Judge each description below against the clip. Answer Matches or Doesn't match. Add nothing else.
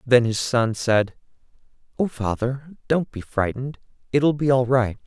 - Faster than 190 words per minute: Doesn't match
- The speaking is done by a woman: Doesn't match